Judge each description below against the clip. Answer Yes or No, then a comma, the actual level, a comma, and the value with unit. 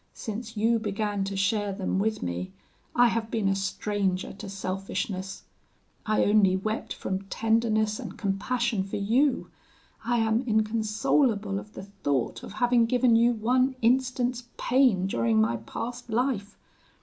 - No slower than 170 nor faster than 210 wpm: No, average, 145 wpm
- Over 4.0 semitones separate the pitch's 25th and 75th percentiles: No, average, 3.3 semitones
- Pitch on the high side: Yes, high, 215 Hz